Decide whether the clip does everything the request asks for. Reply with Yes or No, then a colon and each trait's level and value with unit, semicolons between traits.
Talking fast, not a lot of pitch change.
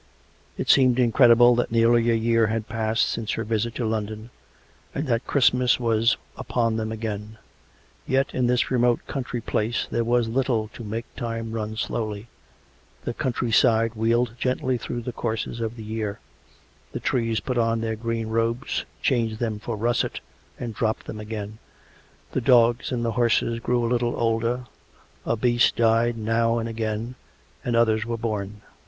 No: average, 165 wpm; narrow, 1.3 semitones